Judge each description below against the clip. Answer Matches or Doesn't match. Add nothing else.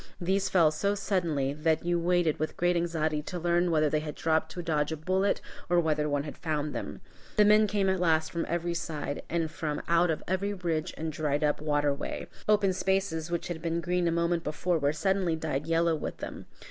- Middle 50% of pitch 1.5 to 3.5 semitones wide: Matches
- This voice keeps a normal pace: Doesn't match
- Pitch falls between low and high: Matches